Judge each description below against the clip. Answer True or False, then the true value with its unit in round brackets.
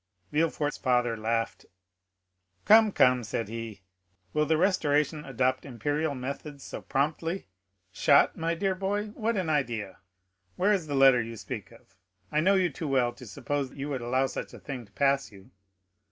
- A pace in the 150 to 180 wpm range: True (170 wpm)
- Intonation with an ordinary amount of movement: True (4.8 semitones)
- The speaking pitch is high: False (140 Hz)